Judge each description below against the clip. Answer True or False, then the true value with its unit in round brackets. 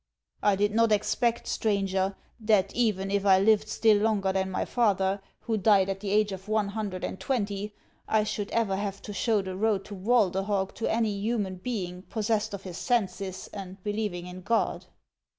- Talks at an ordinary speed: True (185 wpm)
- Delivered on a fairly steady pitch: True (2.1 semitones)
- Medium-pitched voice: False (205 Hz)